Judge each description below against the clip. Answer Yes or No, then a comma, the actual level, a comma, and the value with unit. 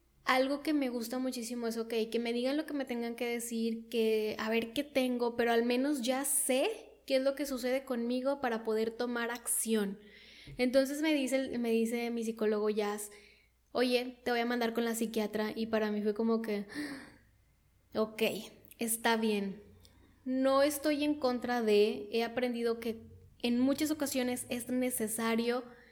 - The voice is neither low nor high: No, high, 240 Hz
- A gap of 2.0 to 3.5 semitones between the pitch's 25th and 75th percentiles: Yes, narrow, 2.5 semitones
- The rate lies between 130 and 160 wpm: No, average, 170 wpm